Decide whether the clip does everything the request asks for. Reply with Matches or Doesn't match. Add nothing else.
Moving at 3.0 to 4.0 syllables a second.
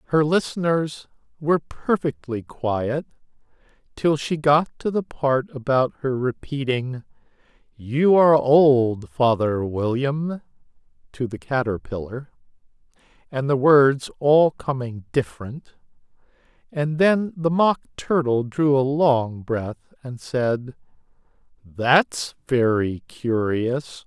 Matches